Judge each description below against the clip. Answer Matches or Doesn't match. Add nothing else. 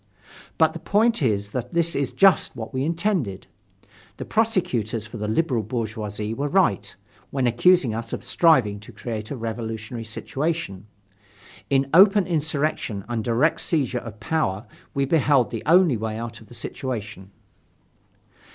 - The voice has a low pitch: Matches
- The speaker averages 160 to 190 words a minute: Doesn't match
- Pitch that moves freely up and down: Matches